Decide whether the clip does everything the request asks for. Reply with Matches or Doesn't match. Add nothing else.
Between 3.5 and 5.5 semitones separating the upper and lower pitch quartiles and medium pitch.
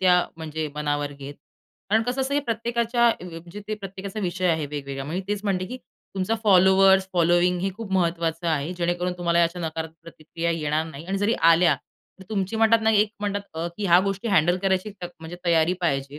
Matches